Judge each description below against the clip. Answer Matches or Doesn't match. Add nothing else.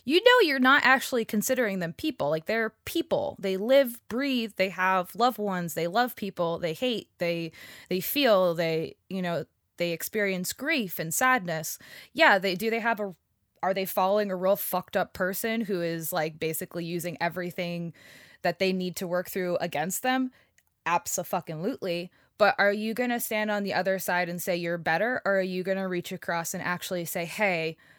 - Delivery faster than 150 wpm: Matches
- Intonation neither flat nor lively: Matches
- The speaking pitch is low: Doesn't match